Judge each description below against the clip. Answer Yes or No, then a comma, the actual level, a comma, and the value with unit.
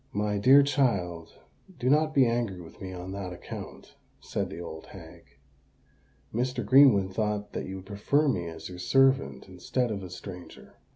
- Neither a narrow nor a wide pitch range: No, wide, 6.2 semitones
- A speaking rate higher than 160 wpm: Yes, average, 170 wpm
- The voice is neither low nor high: No, low, 100 Hz